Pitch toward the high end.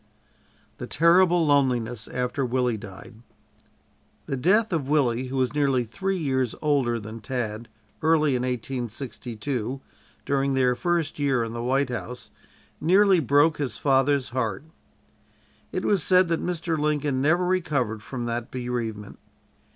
No: low, 130 Hz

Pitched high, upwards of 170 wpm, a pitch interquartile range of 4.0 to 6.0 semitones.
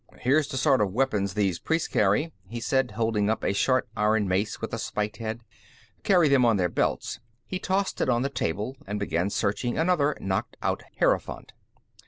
No: low, 115 Hz; average, 190 wpm; average, 5.0 semitones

